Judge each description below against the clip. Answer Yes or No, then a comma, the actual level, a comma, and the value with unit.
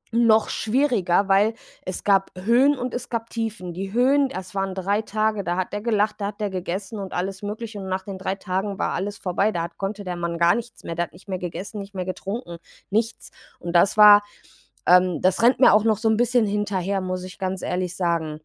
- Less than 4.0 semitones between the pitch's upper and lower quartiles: Yes, average, 2.9 semitones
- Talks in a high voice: Yes, high, 195 Hz